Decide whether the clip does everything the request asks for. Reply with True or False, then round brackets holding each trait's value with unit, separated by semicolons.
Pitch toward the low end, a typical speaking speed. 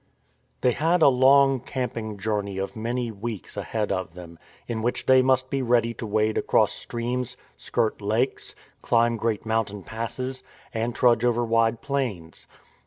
True (115 Hz; 155 wpm)